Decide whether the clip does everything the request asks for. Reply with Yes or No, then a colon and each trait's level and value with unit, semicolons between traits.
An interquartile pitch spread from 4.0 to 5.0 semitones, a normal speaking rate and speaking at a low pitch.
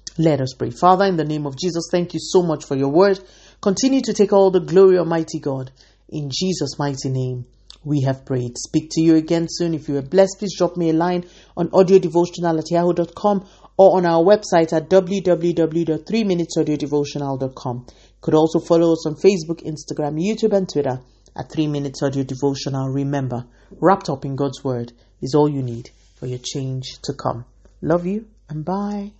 No: average, 4.5 semitones; average, 185 wpm; medium, 160 Hz